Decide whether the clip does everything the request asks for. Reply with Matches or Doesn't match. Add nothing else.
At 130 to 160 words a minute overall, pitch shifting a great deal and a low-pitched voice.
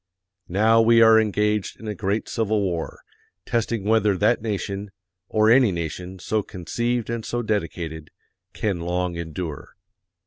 Doesn't match